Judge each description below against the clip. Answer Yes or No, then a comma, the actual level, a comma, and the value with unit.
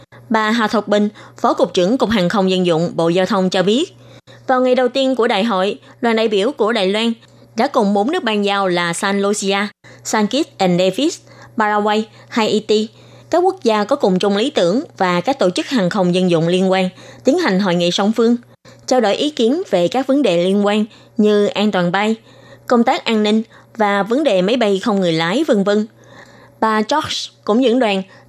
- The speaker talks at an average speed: Yes, average, 215 wpm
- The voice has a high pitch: Yes, high, 210 Hz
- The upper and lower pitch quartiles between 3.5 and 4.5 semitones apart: Yes, average, 3.8 semitones